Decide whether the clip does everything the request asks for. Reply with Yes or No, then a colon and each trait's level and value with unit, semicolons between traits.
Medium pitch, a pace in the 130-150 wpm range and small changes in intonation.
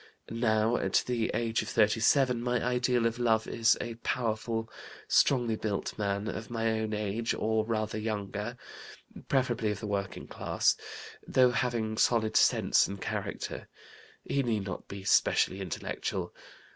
No: low, 110 Hz; average, 145 wpm; narrow, 1.9 semitones